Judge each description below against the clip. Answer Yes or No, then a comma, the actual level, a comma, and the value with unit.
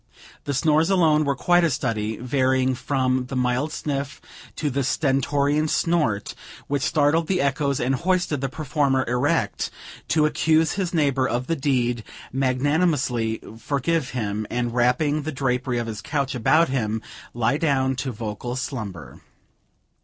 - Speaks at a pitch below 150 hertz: Yes, low, 135 Hz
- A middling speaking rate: Yes, average, 145 wpm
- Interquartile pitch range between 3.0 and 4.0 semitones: Yes, average, 3.4 semitones